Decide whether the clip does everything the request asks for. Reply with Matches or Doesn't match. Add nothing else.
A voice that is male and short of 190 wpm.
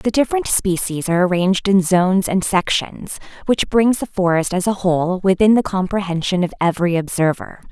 Doesn't match